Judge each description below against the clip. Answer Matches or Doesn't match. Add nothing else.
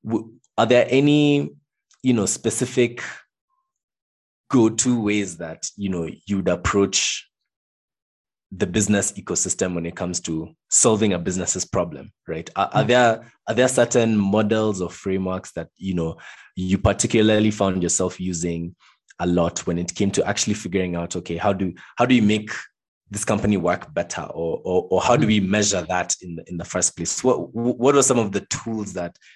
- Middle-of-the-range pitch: Doesn't match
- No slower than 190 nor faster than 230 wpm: Doesn't match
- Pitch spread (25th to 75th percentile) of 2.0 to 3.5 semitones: Doesn't match